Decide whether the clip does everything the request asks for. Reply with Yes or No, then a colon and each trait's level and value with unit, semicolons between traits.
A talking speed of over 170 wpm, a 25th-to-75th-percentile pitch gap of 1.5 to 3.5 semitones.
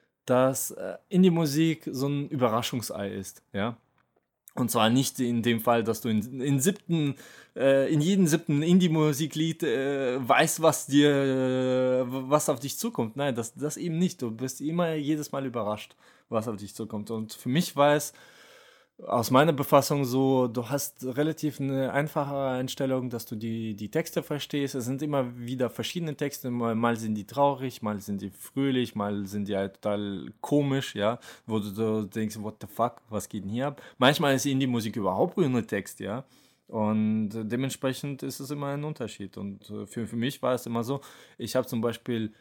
No: average, 185 wpm; average, 4.2 semitones